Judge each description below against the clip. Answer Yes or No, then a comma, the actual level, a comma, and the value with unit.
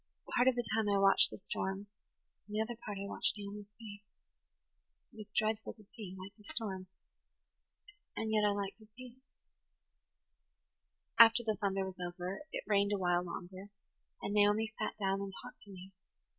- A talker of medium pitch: No, high, 205 Hz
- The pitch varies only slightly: Yes, narrow, 2.0 semitones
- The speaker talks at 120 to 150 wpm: No, average, 180 wpm